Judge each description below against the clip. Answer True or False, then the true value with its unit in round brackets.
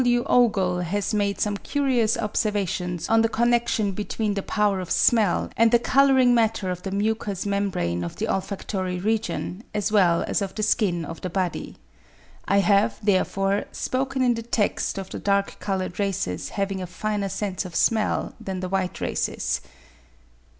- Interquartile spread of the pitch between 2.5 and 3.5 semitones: True (3.0 semitones)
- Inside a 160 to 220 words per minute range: True (170 wpm)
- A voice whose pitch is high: True (200 Hz)